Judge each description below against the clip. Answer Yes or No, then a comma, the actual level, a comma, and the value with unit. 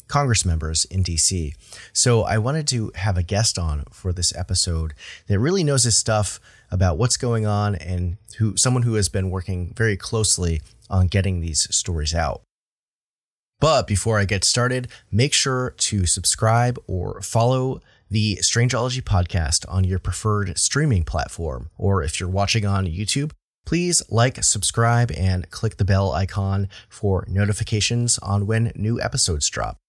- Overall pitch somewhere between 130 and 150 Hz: No, low, 100 Hz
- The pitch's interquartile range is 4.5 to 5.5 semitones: No, average, 4.1 semitones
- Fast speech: No, average, 155 wpm